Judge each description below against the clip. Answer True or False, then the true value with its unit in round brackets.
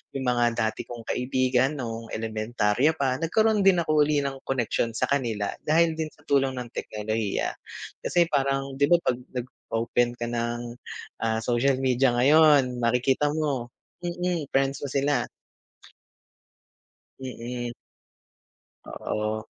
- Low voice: True (125 Hz)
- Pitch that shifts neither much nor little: True (3.3 semitones)